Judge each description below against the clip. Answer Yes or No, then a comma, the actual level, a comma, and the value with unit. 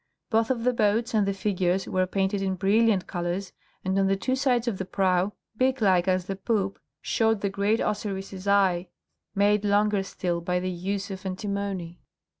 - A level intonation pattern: Yes, narrow, 2.1 semitones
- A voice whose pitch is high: Yes, high, 195 Hz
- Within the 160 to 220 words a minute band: Yes, average, 180 wpm